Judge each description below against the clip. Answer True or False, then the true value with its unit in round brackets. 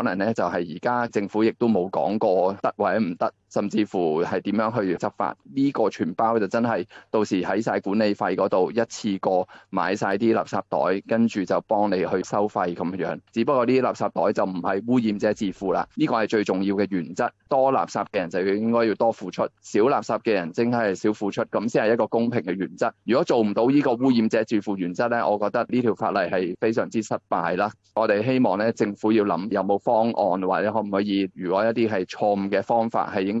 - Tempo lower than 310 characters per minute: False (325 characters per minute)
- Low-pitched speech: True (110 Hz)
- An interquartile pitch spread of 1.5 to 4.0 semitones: True (2.7 semitones)